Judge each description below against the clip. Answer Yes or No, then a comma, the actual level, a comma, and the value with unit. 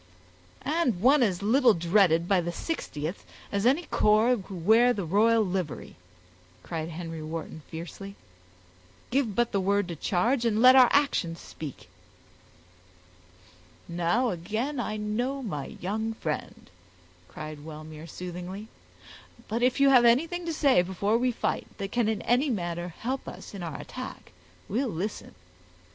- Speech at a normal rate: Yes, average, 145 wpm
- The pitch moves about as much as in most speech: No, wide, 5.9 semitones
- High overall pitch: Yes, high, 205 Hz